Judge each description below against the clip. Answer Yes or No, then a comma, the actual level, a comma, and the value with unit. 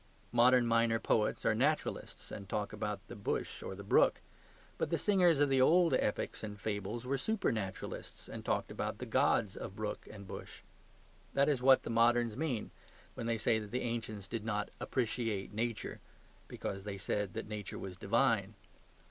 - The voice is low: Yes, low, 115 Hz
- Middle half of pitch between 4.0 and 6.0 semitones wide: No, average, 3.3 semitones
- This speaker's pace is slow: No, average, 175 wpm